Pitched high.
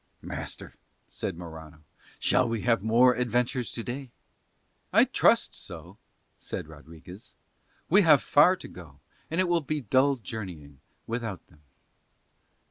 No: low, 115 Hz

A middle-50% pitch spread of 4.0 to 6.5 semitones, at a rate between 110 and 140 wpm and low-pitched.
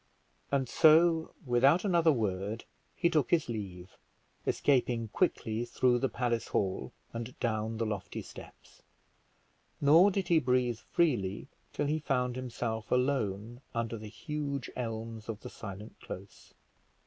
Yes: average, 4.4 semitones; slow, 135 wpm; low, 120 Hz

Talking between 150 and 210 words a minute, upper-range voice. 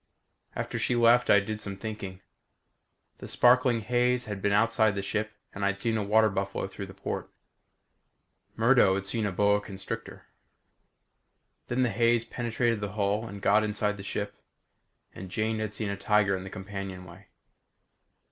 No: average, 165 wpm; low, 105 Hz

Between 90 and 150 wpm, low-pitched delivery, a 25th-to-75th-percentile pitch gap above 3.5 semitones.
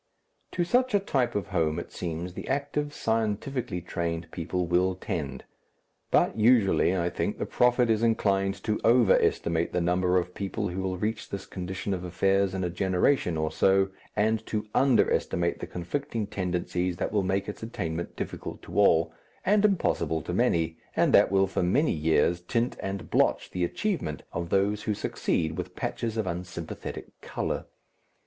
No: average, 170 wpm; very low, 95 Hz; average, 4.2 semitones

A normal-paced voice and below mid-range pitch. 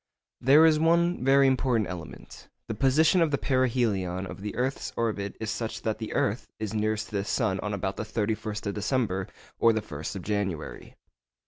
Yes: average, 190 wpm; low, 110 Hz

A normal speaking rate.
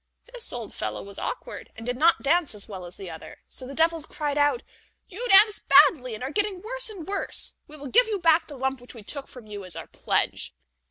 No: fast, 235 wpm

